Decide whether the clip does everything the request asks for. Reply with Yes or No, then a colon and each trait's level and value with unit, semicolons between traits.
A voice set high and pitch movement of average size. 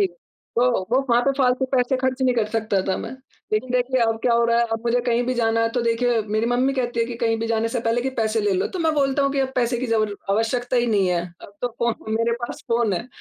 No: high, 235 Hz; narrow, 1.8 semitones